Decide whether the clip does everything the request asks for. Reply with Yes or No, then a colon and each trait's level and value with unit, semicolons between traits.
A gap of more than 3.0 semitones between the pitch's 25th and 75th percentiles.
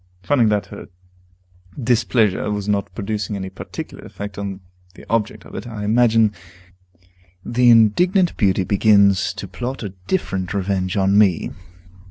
No: average, 2.7 semitones